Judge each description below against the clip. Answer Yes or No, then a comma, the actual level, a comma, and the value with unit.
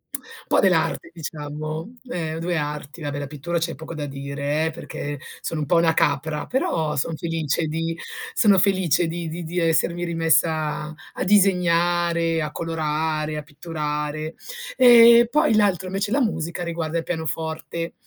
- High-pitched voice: No, medium, 165 Hz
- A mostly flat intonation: Yes, narrow, 2.2 semitones